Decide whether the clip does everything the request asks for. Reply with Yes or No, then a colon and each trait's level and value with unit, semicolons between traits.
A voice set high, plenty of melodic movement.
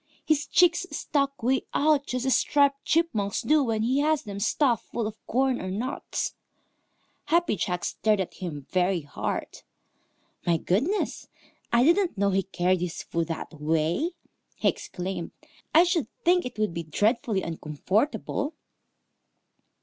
Yes: high, 225 Hz; wide, 7.8 semitones